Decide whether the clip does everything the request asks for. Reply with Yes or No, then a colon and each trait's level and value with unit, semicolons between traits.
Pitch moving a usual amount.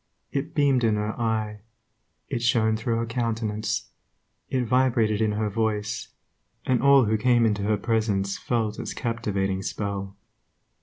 No: narrow, 2.0 semitones